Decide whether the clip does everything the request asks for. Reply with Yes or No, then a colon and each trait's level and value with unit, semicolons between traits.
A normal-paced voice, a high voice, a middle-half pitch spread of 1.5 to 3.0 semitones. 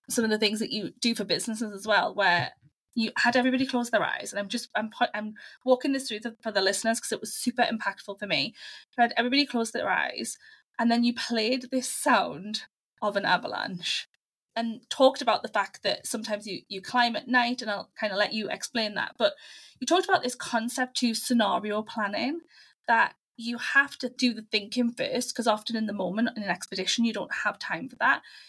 No: fast, 220 wpm; high, 230 Hz; average, 2.7 semitones